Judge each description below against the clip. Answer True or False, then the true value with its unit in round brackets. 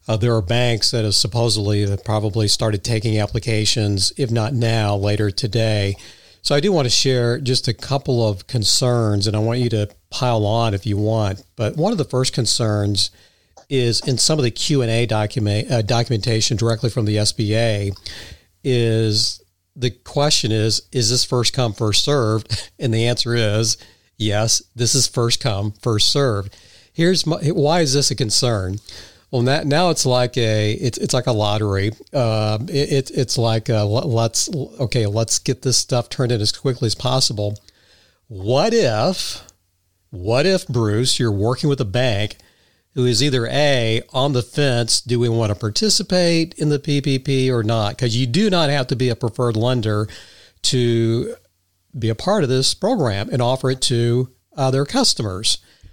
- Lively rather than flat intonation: False (3.5 semitones)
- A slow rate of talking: False (170 wpm)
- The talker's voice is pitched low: True (115 Hz)